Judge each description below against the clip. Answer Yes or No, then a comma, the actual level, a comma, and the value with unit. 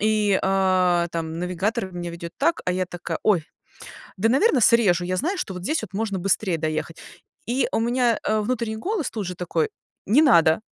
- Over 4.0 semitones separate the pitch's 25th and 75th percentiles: Yes, average, 4.6 semitones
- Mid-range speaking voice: No, high, 195 Hz